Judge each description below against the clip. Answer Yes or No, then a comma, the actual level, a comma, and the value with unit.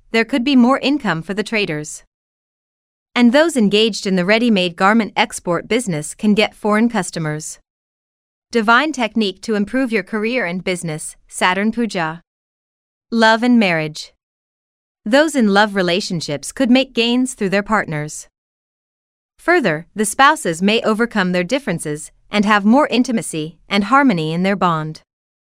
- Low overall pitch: No, high, 210 Hz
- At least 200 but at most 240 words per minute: No, average, 145 wpm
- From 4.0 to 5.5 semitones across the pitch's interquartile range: Yes, average, 5.2 semitones